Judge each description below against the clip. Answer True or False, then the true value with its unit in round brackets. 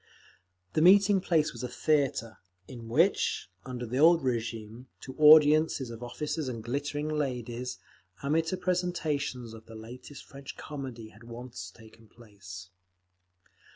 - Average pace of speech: False (130 wpm)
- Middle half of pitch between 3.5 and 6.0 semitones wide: True (4.9 semitones)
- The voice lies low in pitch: True (130 Hz)